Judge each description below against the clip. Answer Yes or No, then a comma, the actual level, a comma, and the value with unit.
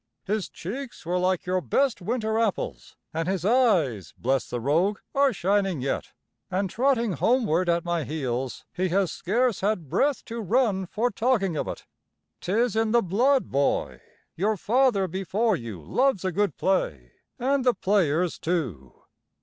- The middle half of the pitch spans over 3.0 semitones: Yes, wide, 5.6 semitones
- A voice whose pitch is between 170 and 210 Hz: Yes, high, 190 Hz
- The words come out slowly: No, average, 160 wpm